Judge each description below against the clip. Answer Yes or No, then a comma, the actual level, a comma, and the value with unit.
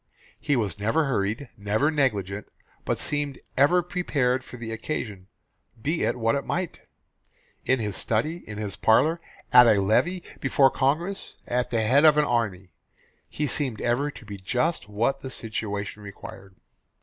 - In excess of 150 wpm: Yes, average, 160 wpm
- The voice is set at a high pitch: No, low, 125 Hz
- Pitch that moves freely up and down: Yes, wide, 5.7 semitones